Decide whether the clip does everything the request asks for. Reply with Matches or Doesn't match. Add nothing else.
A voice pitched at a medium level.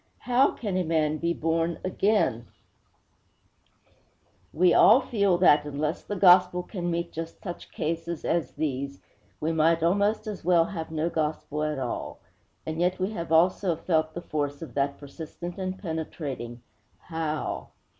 Matches